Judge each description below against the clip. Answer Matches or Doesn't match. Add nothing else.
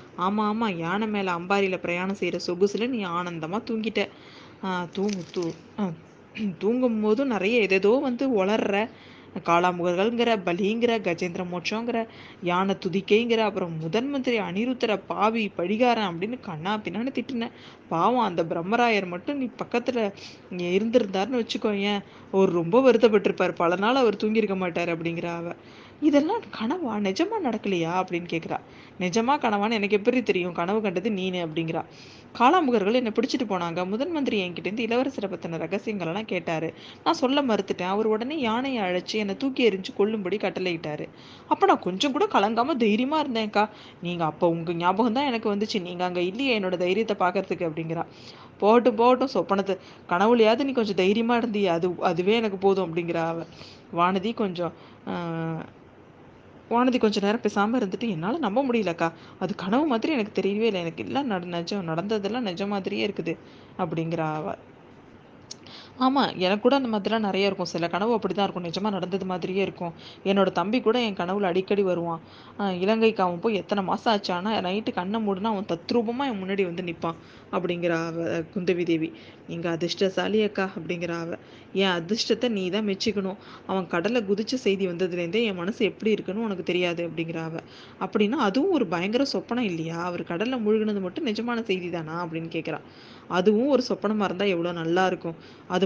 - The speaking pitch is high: Matches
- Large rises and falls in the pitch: Doesn't match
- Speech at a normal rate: Doesn't match